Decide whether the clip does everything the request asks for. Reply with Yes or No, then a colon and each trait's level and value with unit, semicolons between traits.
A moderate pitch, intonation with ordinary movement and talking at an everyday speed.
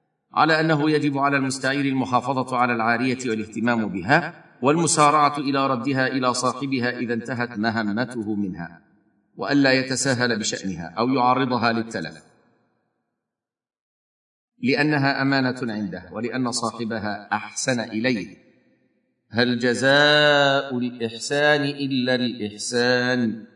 No: low, 125 Hz; average, 3.3 semitones; average, 95 wpm